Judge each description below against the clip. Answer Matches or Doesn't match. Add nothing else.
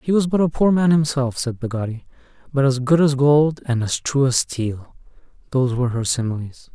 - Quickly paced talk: Doesn't match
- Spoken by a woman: Doesn't match